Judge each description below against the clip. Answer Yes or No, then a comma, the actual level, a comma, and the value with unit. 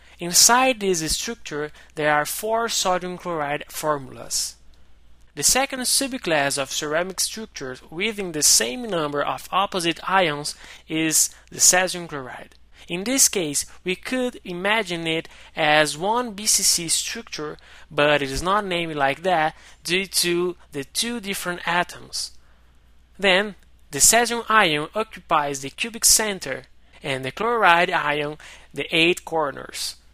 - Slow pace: Yes, slow, 130 wpm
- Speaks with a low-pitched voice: No, medium, 170 Hz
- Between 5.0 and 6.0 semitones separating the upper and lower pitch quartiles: Yes, wide, 5.4 semitones